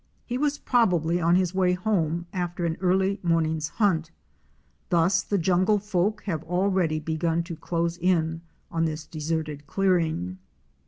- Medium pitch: Yes, medium, 175 Hz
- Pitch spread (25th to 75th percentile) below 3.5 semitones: Yes, average, 2.7 semitones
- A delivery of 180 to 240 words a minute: No, average, 145 wpm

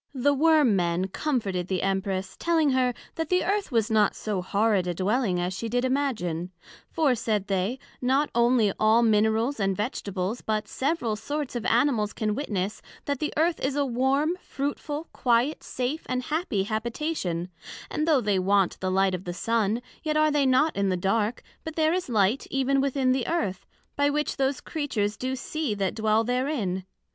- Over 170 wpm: Yes, average, 180 wpm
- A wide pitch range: Yes, wide, 6.1 semitones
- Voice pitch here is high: Yes, high, 235 Hz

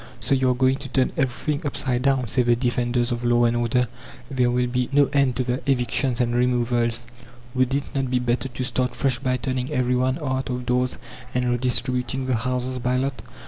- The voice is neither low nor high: No, low, 125 Hz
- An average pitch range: No, narrow, 1.2 semitones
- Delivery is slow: No, fast, 205 wpm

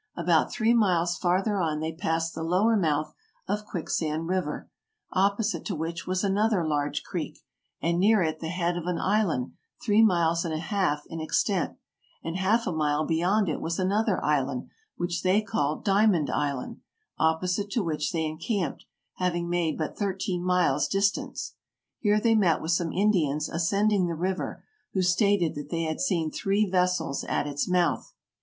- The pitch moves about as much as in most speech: Yes, average, 3.7 semitones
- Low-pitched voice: No, medium, 175 Hz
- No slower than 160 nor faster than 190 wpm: Yes, average, 170 wpm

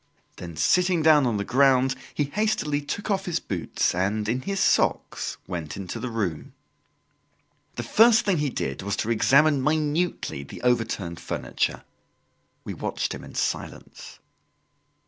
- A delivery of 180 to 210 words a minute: No, average, 145 wpm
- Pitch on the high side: No, low, 130 Hz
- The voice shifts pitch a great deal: Yes, wide, 7.7 semitones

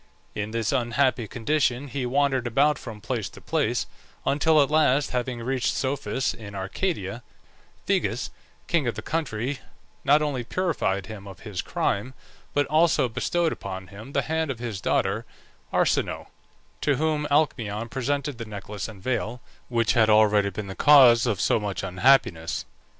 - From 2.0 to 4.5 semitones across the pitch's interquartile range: No, average, 5.0 semitones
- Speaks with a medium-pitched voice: No, low, 120 Hz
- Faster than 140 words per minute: Yes, average, 155 wpm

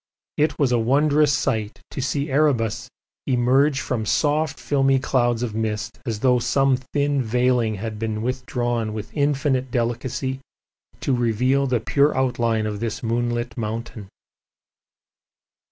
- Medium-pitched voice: No, low, 125 Hz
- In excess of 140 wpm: No, slow, 135 wpm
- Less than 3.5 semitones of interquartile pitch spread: Yes, average, 3.1 semitones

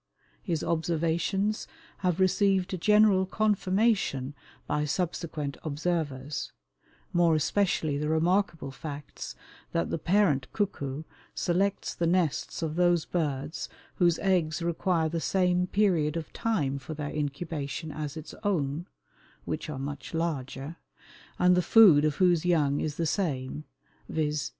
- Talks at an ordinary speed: No, slow, 125 wpm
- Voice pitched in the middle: Yes, medium, 165 Hz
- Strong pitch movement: No, average, 3.5 semitones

